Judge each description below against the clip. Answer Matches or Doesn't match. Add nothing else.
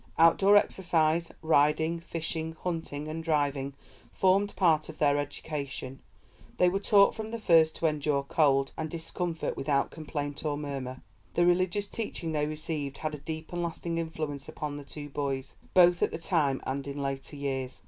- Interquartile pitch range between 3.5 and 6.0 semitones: Doesn't match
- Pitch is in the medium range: Matches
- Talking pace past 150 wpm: Matches